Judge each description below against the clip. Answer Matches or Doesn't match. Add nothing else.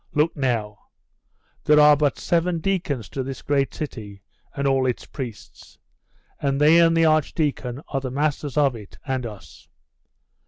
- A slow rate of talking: Doesn't match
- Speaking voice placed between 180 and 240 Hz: Doesn't match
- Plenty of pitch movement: Doesn't match